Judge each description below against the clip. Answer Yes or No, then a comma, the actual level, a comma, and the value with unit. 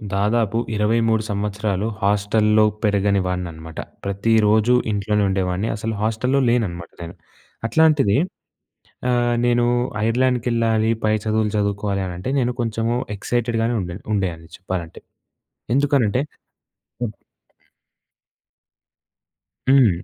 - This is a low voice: Yes, low, 110 Hz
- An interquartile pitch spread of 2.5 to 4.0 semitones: Yes, average, 2.8 semitones